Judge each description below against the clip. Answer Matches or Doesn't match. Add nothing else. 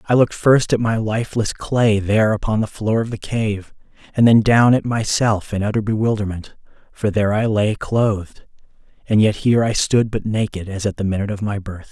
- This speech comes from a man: Matches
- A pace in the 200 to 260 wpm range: Matches